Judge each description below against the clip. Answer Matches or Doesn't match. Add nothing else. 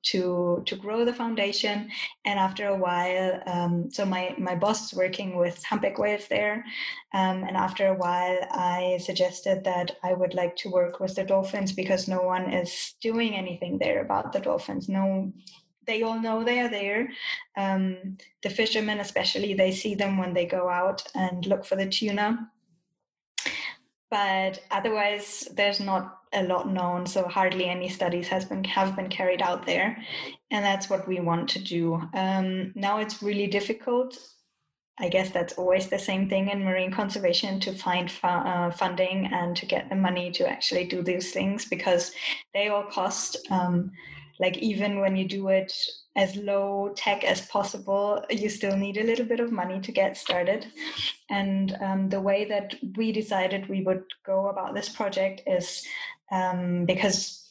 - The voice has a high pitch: Matches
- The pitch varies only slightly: Matches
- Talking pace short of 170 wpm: Doesn't match